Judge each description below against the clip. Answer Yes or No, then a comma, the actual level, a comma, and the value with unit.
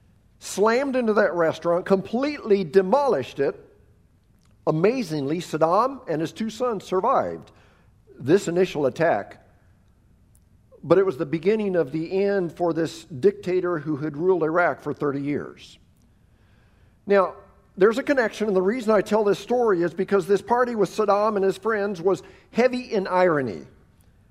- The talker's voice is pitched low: No, medium, 180 Hz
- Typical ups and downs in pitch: No, wide, 6.3 semitones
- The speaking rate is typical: Yes, average, 145 wpm